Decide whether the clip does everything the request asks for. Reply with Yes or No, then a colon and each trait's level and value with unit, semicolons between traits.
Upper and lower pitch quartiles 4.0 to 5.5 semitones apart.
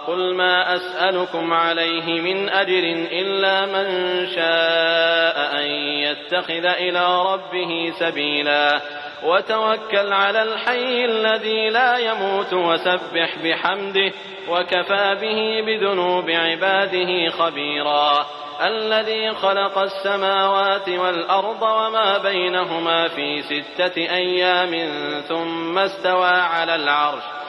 No: average, 2.9 semitones